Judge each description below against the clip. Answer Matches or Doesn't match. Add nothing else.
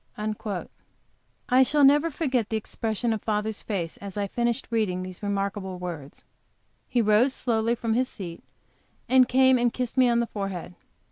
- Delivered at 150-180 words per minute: Matches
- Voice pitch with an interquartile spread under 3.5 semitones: Doesn't match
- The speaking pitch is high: Matches